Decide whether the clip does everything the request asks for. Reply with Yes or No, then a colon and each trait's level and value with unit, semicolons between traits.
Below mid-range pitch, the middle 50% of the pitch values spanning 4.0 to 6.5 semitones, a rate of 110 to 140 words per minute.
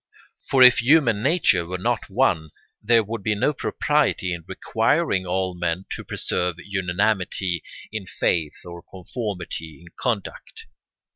Yes: very low, 95 Hz; average, 4.7 semitones; slow, 135 wpm